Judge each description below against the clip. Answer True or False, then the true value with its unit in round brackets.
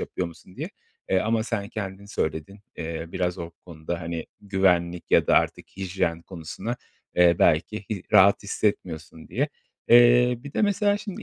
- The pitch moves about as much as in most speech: True (4.3 semitones)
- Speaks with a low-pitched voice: True (95 Hz)